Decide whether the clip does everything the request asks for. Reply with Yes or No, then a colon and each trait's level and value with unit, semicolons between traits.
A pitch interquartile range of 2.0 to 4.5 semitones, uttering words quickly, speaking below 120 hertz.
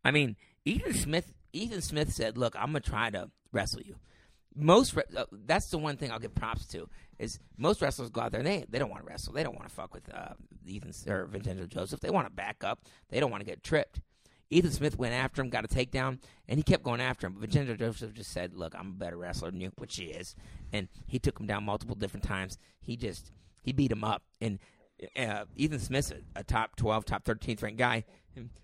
No: average, 5.0 semitones; fast, 240 wpm; low, 110 Hz